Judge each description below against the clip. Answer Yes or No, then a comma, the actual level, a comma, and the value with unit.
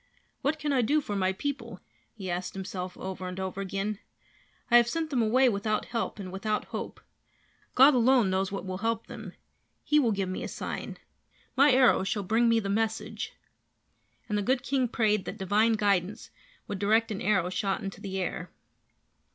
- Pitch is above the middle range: Yes, high, 210 Hz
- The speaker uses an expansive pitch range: No, average, 3.8 semitones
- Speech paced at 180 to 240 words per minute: Yes, average, 185 wpm